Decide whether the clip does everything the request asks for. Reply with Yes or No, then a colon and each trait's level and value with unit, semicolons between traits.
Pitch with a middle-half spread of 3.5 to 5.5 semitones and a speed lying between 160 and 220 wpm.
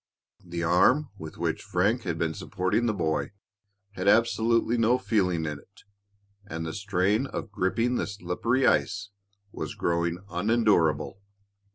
No: average, 5.0 semitones; average, 140 wpm